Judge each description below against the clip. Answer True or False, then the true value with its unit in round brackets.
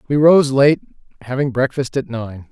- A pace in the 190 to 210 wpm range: False (165 wpm)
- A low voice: True (130 Hz)